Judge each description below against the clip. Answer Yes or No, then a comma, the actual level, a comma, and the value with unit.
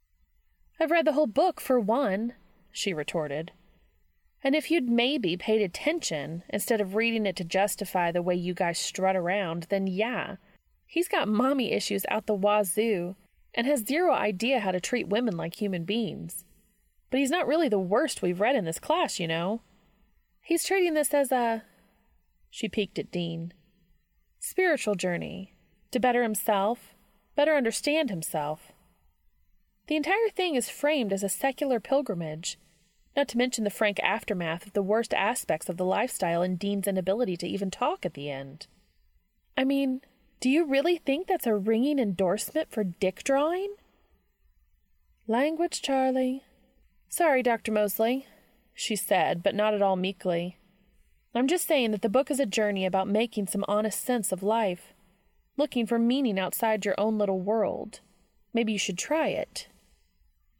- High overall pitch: Yes, high, 210 Hz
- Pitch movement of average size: No, wide, 5.8 semitones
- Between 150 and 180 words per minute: Yes, average, 160 wpm